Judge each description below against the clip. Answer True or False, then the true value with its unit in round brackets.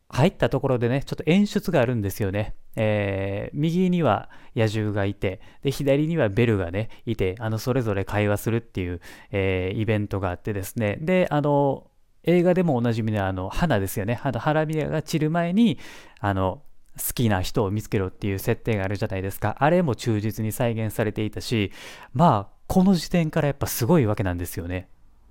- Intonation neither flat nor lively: False (6.4 semitones)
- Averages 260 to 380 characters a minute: False (390 characters per minute)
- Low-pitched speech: True (110 Hz)